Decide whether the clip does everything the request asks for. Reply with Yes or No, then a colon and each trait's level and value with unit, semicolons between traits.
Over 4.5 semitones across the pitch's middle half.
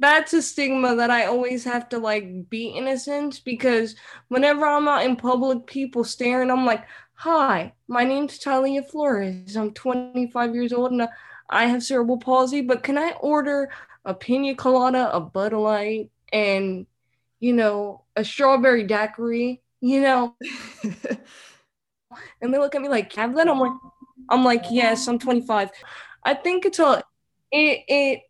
No: average, 3.0 semitones